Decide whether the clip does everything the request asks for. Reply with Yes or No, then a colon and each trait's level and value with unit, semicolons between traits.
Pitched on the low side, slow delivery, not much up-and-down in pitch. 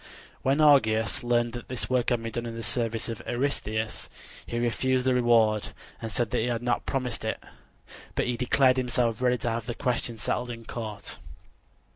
No: low, 120 Hz; average, 190 wpm; narrow, 1.7 semitones